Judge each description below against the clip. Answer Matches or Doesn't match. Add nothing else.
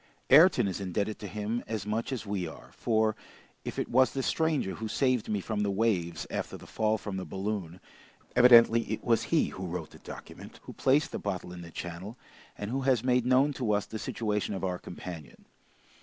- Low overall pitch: Matches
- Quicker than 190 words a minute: Matches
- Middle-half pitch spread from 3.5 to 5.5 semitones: Matches